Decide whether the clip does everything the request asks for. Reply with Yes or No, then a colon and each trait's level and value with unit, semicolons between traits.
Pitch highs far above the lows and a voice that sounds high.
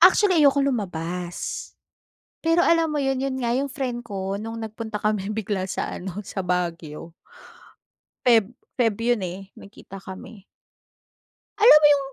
Yes: wide, 6.0 semitones; high, 220 Hz